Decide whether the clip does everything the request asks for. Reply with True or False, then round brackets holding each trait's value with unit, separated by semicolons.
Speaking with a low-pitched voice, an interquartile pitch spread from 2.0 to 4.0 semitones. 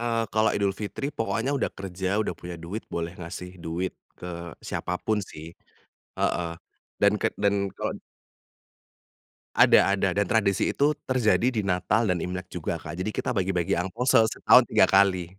True (95 Hz; 3.5 semitones)